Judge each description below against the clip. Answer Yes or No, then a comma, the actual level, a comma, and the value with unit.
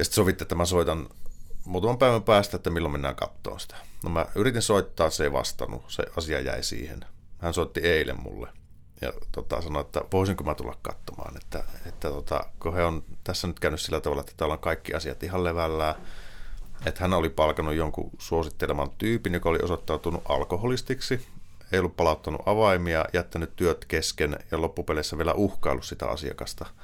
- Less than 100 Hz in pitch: Yes, very low, 85 Hz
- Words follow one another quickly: Yes, fast, 180 wpm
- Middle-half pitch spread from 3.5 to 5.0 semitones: No, average, 2.9 semitones